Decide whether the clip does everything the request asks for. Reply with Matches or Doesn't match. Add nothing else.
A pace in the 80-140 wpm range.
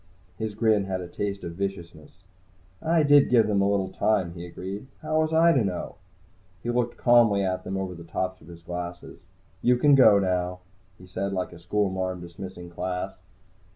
Doesn't match